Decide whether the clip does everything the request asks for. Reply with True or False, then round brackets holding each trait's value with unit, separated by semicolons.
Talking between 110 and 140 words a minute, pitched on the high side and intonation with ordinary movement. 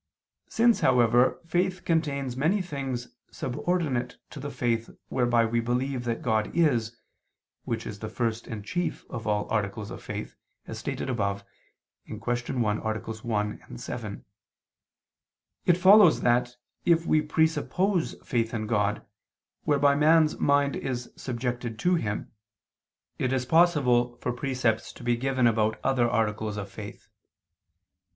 False (135 wpm; 120 Hz; 4.3 semitones)